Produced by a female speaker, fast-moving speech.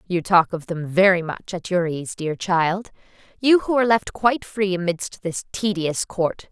No: female; average, 185 wpm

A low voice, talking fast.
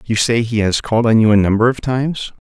Yes: low, 115 Hz; fast, 265 wpm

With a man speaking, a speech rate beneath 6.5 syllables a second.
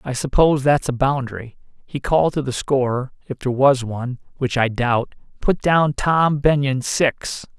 Yes: male; 4.8 syllables/s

